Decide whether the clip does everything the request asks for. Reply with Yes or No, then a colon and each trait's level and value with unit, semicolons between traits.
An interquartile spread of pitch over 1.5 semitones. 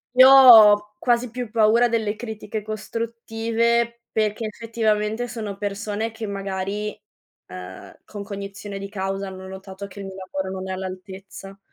Yes: narrow, 2.6 semitones